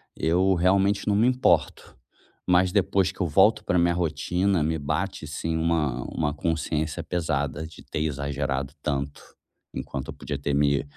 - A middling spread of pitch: Yes, average, 3.9 semitones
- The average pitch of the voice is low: Yes, very low, 80 Hz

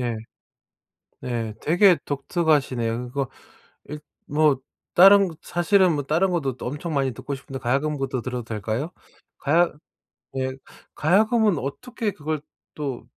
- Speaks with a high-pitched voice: No, medium, 145 Hz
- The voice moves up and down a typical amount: Yes, average, 4.9 semitones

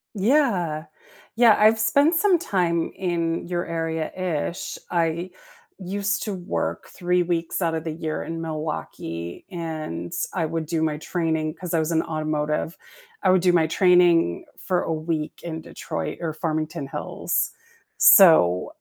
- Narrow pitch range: Yes, narrow, 2.3 semitones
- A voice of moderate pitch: Yes, medium, 165 Hz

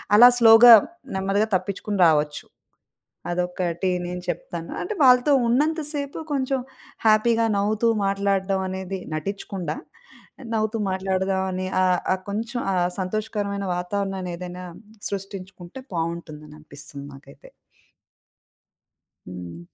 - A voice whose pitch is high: Yes, high, 195 Hz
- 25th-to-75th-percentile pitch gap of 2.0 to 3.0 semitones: No, average, 3.4 semitones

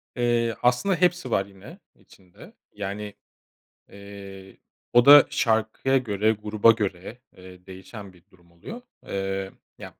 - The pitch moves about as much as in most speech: Yes, average, 3.7 semitones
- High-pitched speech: No, low, 105 Hz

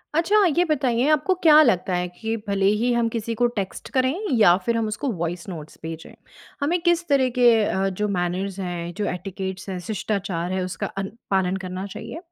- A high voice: Yes, high, 205 Hz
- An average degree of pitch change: No, wide, 6.0 semitones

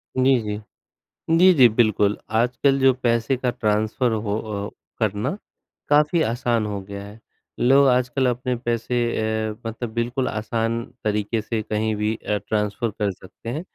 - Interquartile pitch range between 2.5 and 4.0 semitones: Yes, average, 2.9 semitones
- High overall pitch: No, low, 115 Hz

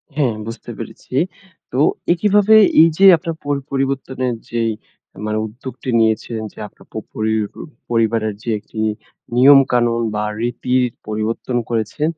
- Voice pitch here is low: Yes, low, 120 Hz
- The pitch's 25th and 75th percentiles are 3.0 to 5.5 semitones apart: Yes, average, 3.4 semitones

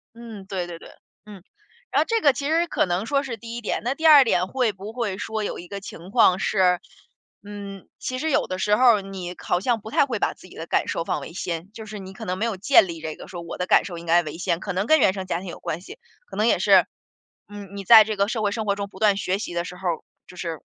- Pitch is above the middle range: Yes, high, 200 Hz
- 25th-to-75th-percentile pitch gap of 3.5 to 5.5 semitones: Yes, average, 3.8 semitones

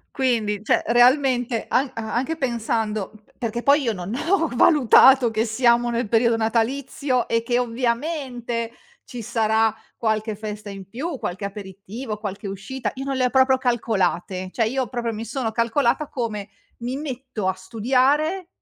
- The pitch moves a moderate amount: Yes, average, 3.3 semitones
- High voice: Yes, high, 235 Hz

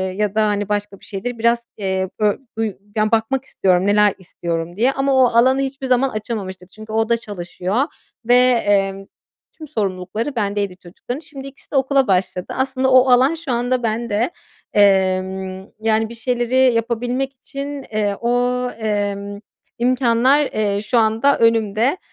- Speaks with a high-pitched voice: Yes, high, 225 Hz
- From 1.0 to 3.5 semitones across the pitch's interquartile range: No, average, 4.0 semitones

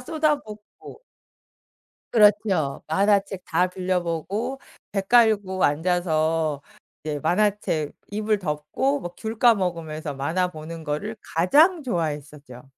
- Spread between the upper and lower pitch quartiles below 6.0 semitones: Yes, average, 5.3 semitones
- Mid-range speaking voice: Yes, medium, 180 Hz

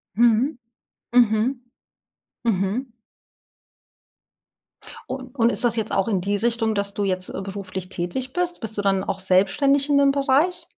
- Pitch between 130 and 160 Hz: No, high, 225 Hz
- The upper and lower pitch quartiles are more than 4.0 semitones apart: Yes, average, 5.0 semitones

